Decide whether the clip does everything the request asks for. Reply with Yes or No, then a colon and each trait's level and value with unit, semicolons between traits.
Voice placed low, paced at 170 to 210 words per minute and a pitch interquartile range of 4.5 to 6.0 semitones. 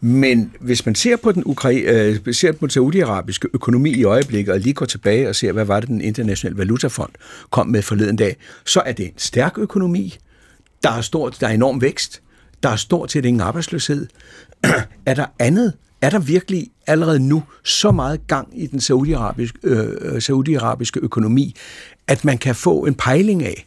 Yes: low, 130 Hz; average, 190 wpm; average, 4.9 semitones